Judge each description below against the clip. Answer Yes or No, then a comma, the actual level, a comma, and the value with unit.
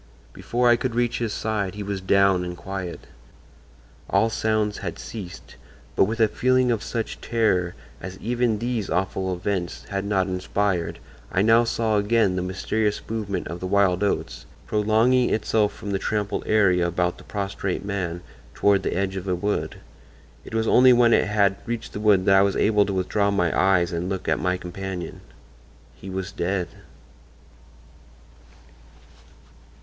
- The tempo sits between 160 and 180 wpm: Yes, average, 165 wpm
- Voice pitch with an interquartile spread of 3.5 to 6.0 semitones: No, average, 2.8 semitones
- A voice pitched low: Yes, low, 100 Hz